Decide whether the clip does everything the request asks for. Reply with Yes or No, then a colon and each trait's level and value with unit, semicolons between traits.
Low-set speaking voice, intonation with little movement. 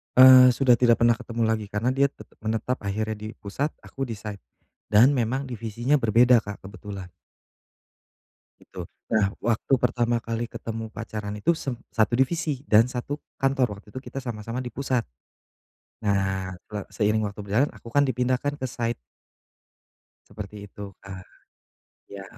No: low, 115 Hz; average, 3.4 semitones